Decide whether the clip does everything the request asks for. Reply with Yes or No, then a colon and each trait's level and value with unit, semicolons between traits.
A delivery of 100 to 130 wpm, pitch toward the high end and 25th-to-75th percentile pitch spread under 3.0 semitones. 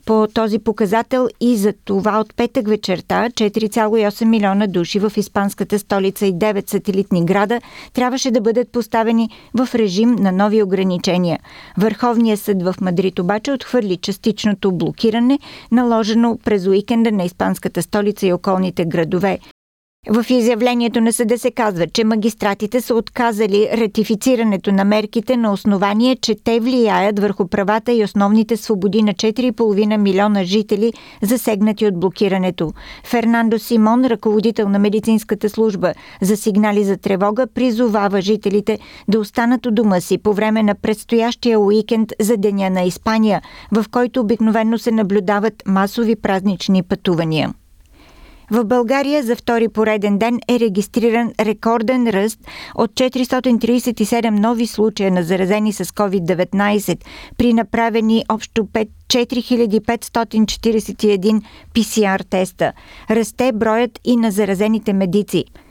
Yes: average, 125 wpm; high, 220 Hz; narrow, 2.4 semitones